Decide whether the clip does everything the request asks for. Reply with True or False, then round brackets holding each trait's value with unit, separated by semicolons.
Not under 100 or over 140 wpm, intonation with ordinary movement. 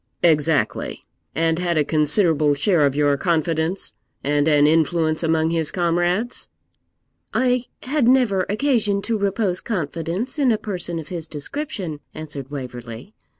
True (135 wpm; 5.0 semitones)